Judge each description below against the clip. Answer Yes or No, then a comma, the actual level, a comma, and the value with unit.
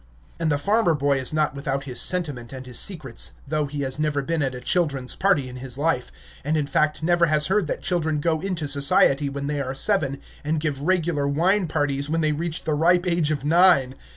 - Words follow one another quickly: Yes, fast, 220 wpm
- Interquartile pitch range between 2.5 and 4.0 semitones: Yes, average, 3.2 semitones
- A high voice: No, medium, 150 Hz